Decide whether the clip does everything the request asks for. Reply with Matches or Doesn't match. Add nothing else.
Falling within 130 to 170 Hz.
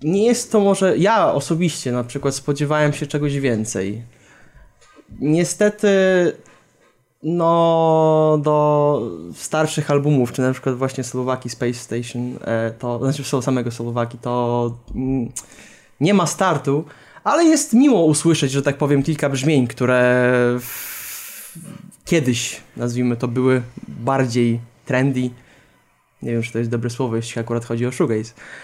Matches